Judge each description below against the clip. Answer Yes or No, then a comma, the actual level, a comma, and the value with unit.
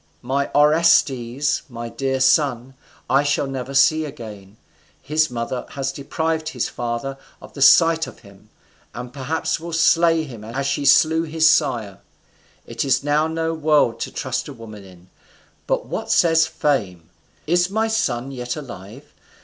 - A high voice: No, low, 135 Hz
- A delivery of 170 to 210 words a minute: No, average, 155 wpm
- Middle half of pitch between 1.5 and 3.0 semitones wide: No, average, 4.8 semitones